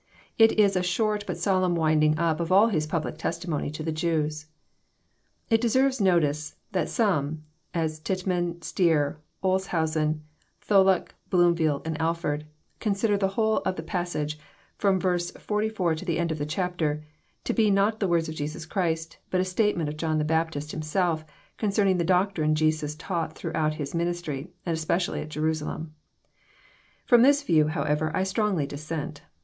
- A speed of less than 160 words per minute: No, average, 165 wpm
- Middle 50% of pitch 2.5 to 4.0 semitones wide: Yes, average, 3.5 semitones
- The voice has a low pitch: No, medium, 170 Hz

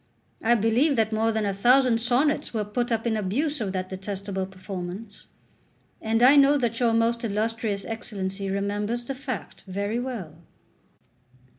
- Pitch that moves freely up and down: No, average, 3.3 semitones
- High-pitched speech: Yes, high, 225 Hz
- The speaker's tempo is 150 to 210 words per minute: Yes, average, 155 wpm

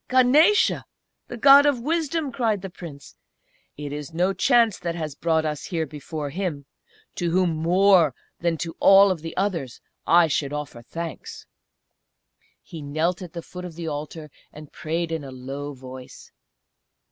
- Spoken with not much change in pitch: No, average, 4.6 semitones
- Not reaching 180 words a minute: Yes, average, 160 wpm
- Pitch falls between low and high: Yes, medium, 165 Hz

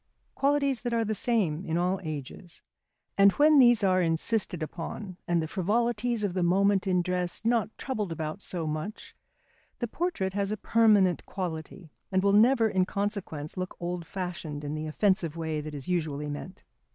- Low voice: No, medium, 185 Hz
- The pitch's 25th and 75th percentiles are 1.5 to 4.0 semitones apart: No, average, 4.6 semitones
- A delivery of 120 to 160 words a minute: No, average, 175 wpm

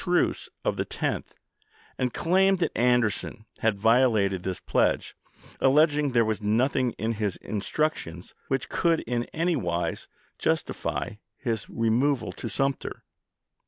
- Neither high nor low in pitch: No, low, 120 Hz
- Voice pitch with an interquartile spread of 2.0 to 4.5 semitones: No, average, 5.0 semitones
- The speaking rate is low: Yes, slow, 125 wpm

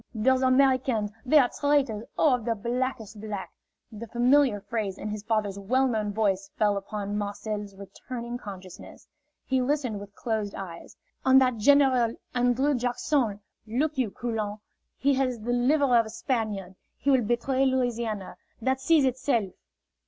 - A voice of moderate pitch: No, high, 235 Hz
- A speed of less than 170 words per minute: Yes, average, 160 wpm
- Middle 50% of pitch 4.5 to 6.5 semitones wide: No, average, 3.9 semitones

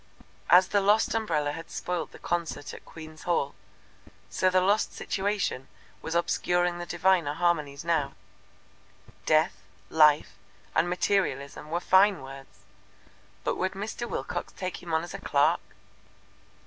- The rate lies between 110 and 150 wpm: Yes, slow, 135 wpm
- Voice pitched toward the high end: No, medium, 175 Hz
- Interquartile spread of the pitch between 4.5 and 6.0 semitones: No, average, 3.4 semitones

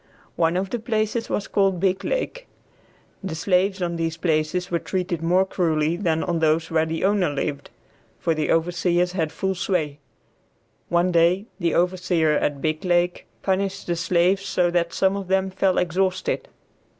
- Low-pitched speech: No, medium, 175 Hz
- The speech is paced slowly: No, average, 160 wpm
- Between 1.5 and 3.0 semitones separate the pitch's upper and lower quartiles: Yes, narrow, 2.6 semitones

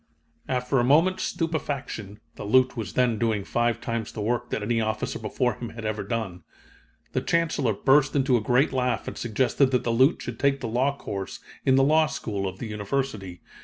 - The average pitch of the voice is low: Yes, low, 120 Hz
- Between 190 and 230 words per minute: Yes, average, 200 wpm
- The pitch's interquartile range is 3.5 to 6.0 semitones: Yes, average, 3.8 semitones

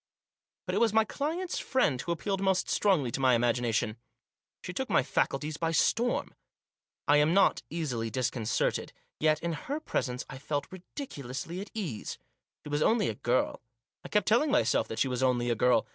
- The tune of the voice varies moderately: No, wide, 8.3 semitones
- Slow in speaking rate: No, average, 185 wpm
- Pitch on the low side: No, medium, 150 Hz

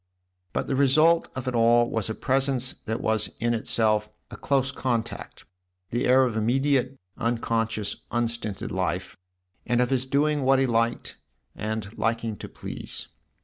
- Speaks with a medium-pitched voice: No, low, 120 Hz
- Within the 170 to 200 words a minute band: No, average, 150 wpm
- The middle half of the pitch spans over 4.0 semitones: No, average, 2.8 semitones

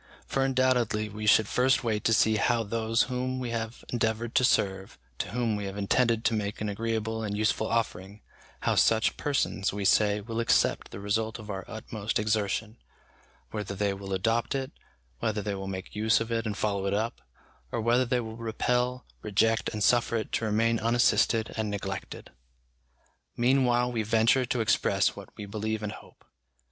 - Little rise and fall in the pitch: Yes, narrow, 2.1 semitones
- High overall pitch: No, low, 110 Hz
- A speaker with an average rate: Yes, average, 180 wpm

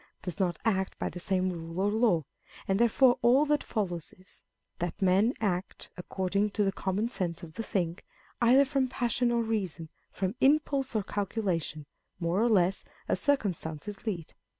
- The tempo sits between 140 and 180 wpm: Yes, average, 170 wpm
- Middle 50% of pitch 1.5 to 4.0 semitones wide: No, average, 4.6 semitones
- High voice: Yes, high, 195 Hz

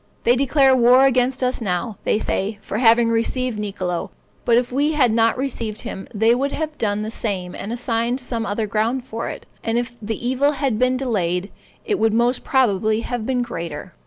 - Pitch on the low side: No, high, 235 Hz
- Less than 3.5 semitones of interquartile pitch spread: Yes, average, 3.0 semitones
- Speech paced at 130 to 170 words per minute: No, average, 195 wpm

